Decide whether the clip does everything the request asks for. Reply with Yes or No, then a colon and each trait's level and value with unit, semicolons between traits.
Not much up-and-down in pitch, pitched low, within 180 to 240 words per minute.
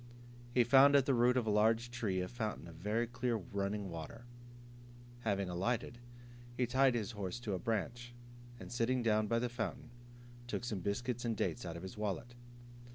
No: average, 3.1 semitones; low, 115 Hz; average, 185 wpm